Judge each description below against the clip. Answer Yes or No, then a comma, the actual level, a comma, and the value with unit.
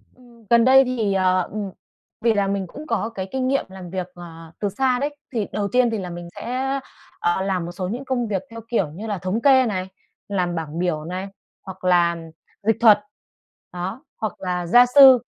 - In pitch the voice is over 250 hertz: No, high, 200 Hz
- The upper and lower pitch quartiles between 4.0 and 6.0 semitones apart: Yes, average, 5.0 semitones